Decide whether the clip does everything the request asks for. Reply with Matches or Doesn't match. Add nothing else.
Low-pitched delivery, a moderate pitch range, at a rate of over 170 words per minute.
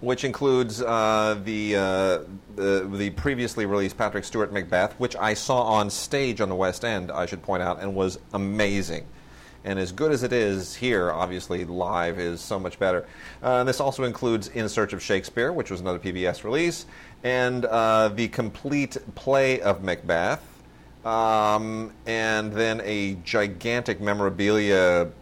Doesn't match